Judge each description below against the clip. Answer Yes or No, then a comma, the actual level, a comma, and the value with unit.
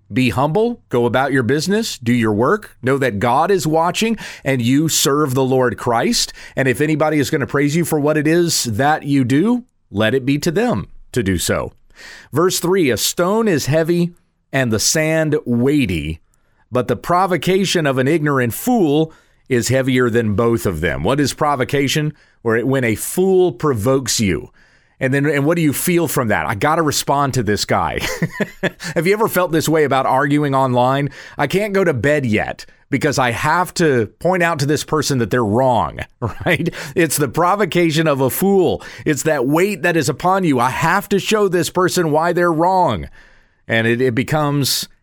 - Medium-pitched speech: Yes, medium, 145 Hz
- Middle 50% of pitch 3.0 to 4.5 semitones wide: No, average, 5.3 semitones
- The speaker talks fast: No, average, 195 wpm